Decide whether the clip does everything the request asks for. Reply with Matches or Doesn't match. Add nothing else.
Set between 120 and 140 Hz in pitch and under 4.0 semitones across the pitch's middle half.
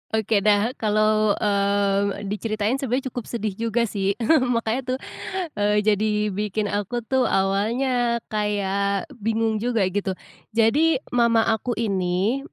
Doesn't match